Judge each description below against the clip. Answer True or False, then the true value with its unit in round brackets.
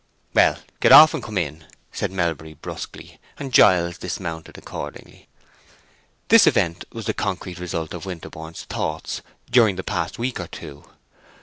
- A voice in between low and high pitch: False (90 Hz)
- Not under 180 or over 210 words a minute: False (145 wpm)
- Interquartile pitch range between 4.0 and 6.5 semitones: True (4.6 semitones)